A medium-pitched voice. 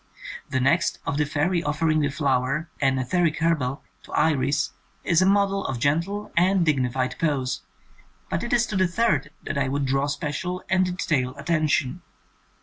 Yes: medium, 150 Hz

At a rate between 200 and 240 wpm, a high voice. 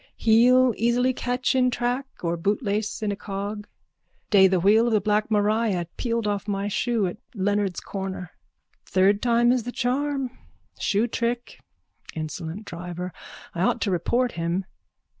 No: average, 150 wpm; high, 210 Hz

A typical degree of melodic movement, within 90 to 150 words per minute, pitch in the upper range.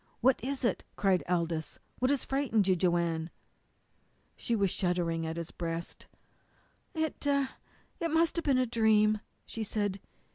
No: wide, 7.4 semitones; average, 145 wpm; high, 210 Hz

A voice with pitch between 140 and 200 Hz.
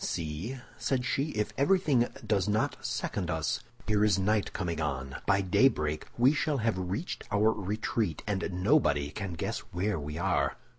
No: low, 100 Hz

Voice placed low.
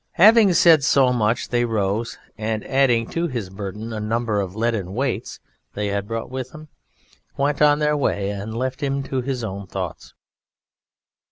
Yes: low, 120 Hz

